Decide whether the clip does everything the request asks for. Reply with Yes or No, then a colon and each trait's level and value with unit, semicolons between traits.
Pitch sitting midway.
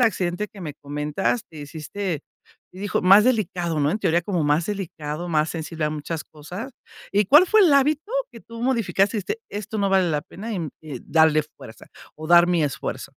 Yes: medium, 175 Hz